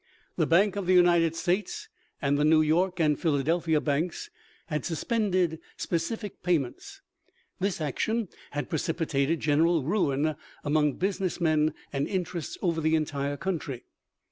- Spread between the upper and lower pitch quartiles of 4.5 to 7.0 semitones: No, average, 3.3 semitones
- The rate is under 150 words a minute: Yes, average, 140 wpm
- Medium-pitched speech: Yes, medium, 165 Hz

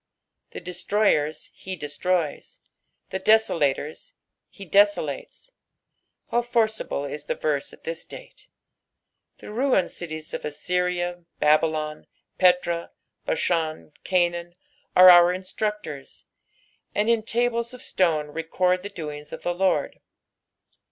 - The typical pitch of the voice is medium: Yes, medium, 175 Hz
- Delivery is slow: Yes, slow, 115 wpm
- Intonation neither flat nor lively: Yes, average, 4.6 semitones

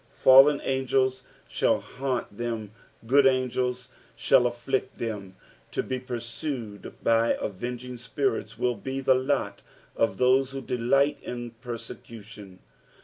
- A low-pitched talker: Yes, low, 125 Hz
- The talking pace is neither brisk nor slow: No, slow, 120 wpm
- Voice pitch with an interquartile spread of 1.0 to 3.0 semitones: Yes, narrow, 2.4 semitones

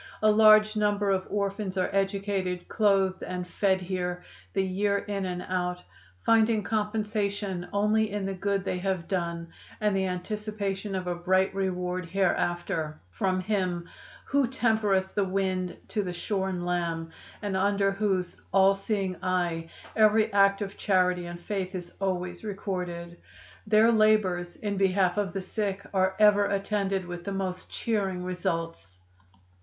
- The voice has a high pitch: Yes, high, 195 Hz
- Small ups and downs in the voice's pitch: Yes, narrow, 2.2 semitones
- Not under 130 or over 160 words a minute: Yes, average, 150 wpm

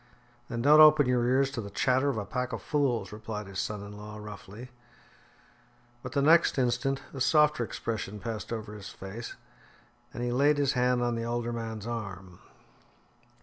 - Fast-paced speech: No, average, 180 wpm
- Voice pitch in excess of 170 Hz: No, low, 120 Hz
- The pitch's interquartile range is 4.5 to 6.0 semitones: No, average, 3.9 semitones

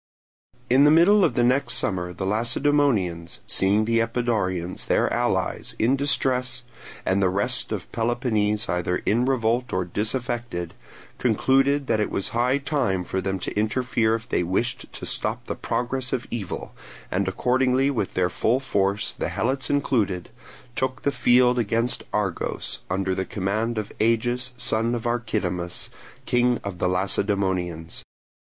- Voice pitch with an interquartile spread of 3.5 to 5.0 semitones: Yes, average, 4.7 semitones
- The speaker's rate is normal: Yes, average, 150 wpm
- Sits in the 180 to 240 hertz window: No, low, 115 Hz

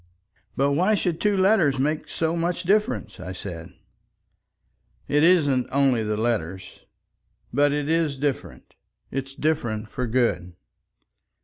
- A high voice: No, medium, 140 Hz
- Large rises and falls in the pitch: Yes, wide, 5.7 semitones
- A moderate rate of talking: No, slow, 125 wpm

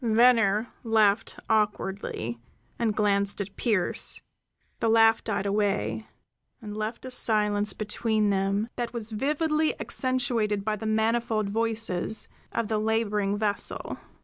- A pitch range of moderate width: No, narrow, 1.9 semitones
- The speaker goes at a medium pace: No, slow, 120 wpm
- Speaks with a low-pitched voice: No, high, 215 Hz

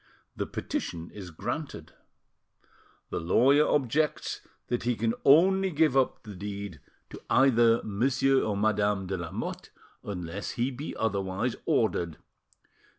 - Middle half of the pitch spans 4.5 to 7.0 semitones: Yes, wide, 5.4 semitones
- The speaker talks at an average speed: No, slow, 125 wpm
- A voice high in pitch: No, low, 110 Hz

